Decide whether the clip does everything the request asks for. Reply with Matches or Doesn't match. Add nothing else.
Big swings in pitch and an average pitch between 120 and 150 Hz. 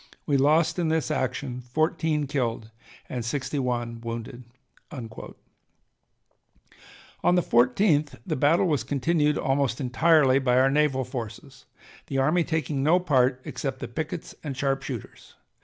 Doesn't match